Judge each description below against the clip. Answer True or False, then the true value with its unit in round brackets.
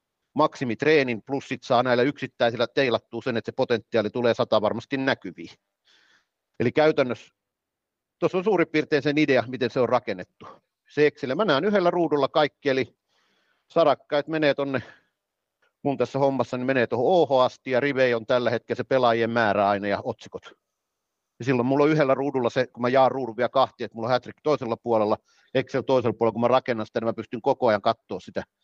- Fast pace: True (190 wpm)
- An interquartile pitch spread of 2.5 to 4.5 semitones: True (3.1 semitones)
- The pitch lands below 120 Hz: False (125 Hz)